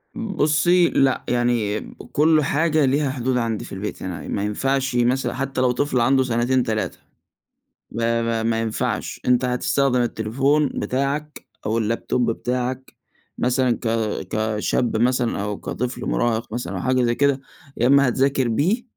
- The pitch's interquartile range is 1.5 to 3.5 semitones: Yes, average, 3.0 semitones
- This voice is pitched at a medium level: No, low, 125 Hz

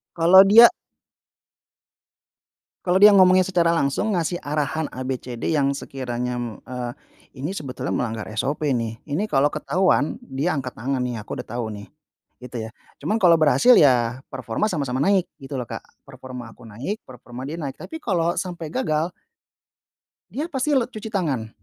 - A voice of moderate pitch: Yes, medium, 145 Hz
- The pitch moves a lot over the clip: Yes, wide, 6.5 semitones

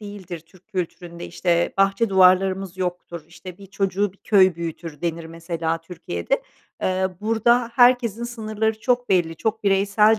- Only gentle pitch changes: No, average, 3.8 semitones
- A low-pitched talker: No, high, 190 Hz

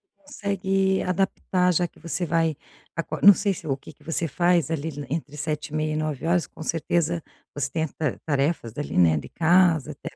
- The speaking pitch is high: No, medium, 165 Hz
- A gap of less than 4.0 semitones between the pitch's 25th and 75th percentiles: Yes, average, 3.0 semitones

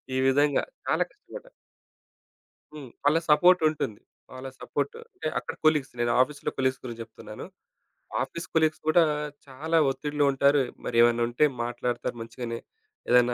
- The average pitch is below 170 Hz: Yes, low, 135 Hz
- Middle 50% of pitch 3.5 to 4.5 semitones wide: Yes, average, 3.9 semitones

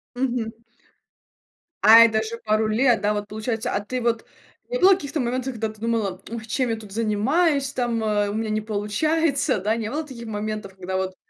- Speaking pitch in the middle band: No, high, 225 Hz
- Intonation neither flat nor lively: Yes, average, 3.1 semitones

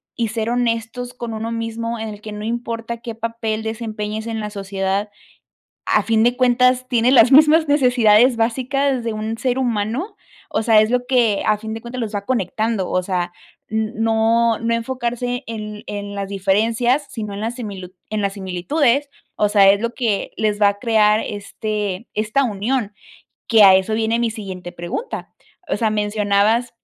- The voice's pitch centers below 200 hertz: No, high, 225 Hz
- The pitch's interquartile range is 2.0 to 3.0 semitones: Yes, narrow, 2.4 semitones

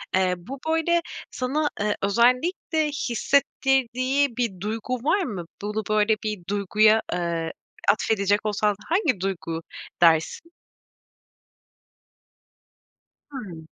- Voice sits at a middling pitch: No, high, 220 Hz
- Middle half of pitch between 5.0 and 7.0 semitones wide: Yes, wide, 5.4 semitones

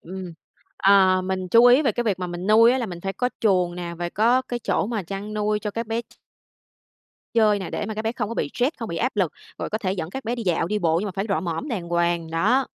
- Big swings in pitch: No, average, 4.3 semitones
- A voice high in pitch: Yes, high, 205 Hz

